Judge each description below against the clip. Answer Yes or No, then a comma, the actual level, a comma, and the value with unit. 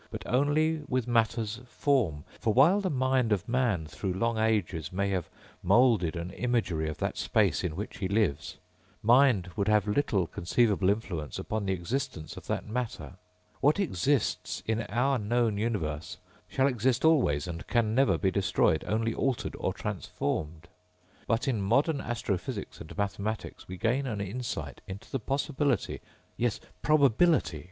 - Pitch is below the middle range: Yes, low, 110 Hz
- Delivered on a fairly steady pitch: No, wide, 5.6 semitones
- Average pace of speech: Yes, average, 155 wpm